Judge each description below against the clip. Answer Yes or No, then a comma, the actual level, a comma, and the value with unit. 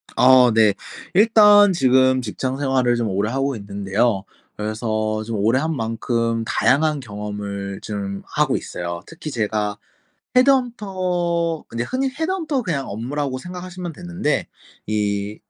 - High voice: No, low, 130 Hz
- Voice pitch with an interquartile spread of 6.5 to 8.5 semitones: Yes, wide, 8.2 semitones